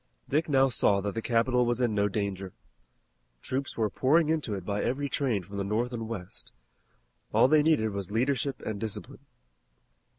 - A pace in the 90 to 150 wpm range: No, average, 175 wpm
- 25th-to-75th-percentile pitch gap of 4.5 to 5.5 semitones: Yes, average, 4.8 semitones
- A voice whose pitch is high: No, low, 115 Hz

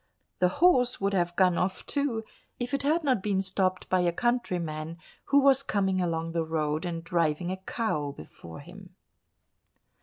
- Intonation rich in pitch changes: Yes, wide, 6.2 semitones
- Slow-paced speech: No, average, 170 wpm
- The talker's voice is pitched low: No, medium, 185 Hz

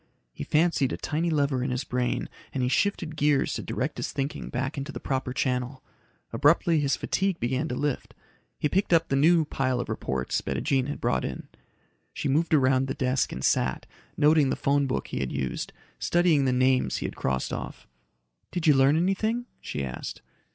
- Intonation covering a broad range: No, average, 3.5 semitones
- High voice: No, medium, 140 Hz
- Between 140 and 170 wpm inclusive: No, average, 195 wpm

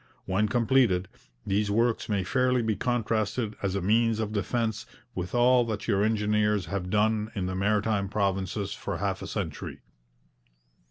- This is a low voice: Yes, low, 105 Hz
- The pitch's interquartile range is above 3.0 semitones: No, narrow, 2.4 semitones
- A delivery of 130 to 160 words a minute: Yes, average, 155 wpm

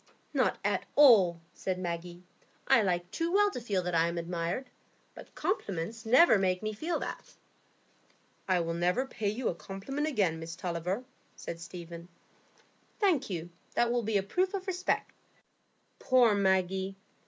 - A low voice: No, high, 195 Hz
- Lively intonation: Yes, wide, 6.4 semitones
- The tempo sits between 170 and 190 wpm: No, average, 155 wpm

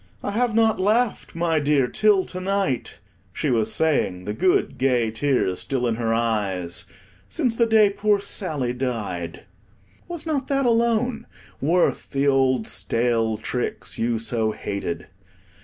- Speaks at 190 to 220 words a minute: No, average, 145 wpm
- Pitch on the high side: No, low, 135 Hz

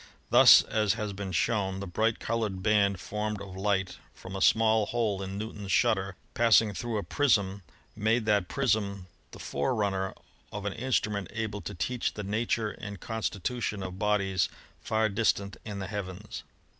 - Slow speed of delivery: No, average, 170 wpm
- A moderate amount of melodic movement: No, narrow, 2.1 semitones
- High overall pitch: No, low, 105 Hz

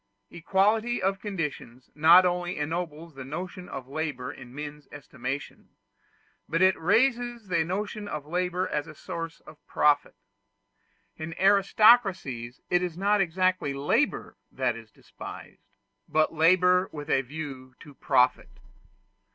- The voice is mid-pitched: Yes, medium, 165 Hz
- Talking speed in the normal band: No, slow, 130 wpm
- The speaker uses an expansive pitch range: No, average, 4.3 semitones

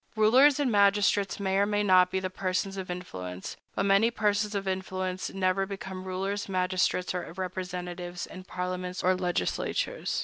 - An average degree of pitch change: No, narrow, 1.7 semitones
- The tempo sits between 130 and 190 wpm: Yes, average, 150 wpm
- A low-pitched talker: No, medium, 185 Hz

